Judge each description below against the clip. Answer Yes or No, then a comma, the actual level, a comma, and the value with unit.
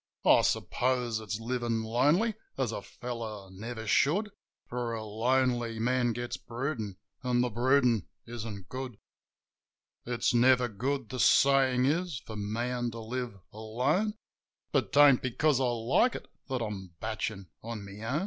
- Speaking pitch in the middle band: No, low, 120 Hz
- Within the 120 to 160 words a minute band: Yes, average, 145 wpm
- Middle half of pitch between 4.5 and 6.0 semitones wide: No, average, 2.7 semitones